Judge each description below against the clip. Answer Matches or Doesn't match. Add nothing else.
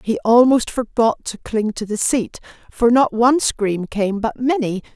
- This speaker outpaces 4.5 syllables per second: Doesn't match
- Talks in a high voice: Matches